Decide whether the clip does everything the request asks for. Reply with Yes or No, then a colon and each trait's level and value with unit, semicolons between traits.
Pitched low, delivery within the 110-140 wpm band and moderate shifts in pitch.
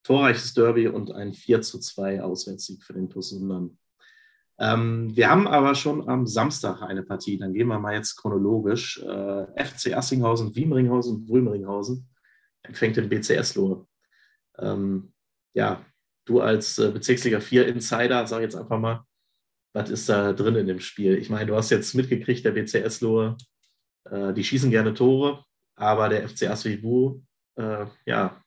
No: low, 110 Hz; average, 155 wpm; average, 3.7 semitones